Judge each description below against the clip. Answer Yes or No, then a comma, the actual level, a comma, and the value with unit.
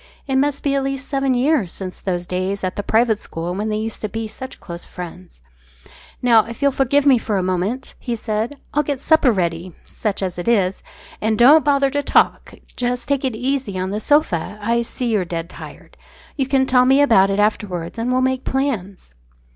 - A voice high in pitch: Yes, high, 230 Hz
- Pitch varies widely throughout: Yes, wide, 5.9 semitones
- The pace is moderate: No, fast, 210 wpm